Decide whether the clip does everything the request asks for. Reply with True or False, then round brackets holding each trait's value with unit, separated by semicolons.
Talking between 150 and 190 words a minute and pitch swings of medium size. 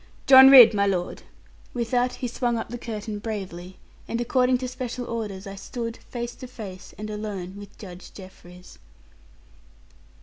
True (160 wpm; 3.8 semitones)